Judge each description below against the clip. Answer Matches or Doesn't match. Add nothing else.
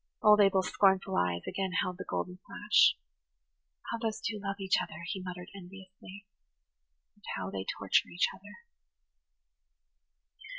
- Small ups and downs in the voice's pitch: Matches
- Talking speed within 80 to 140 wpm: Matches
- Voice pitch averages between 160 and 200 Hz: Matches